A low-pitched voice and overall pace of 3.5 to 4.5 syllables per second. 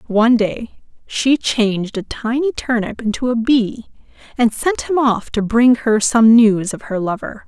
No: high, 230 Hz; 4.3 syllables/s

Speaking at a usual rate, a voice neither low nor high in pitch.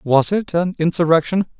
Yes: average, 150 wpm; medium, 170 Hz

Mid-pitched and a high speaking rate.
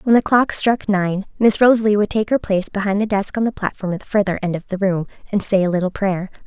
No: high, 200 Hz; fast, 270 wpm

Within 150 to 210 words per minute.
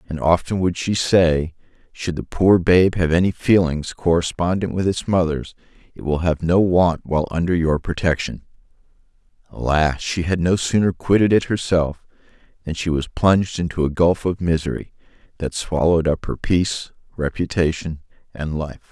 Yes: average, 160 wpm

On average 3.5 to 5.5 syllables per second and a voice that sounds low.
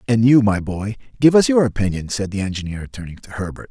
No: 6.0 syllables/s; low, 110 Hz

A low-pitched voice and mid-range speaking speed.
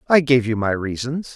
No: low, 125 Hz; fast, 220 wpm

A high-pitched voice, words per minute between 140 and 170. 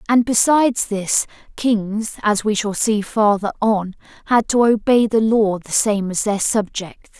Yes: high, 215 Hz; average, 165 wpm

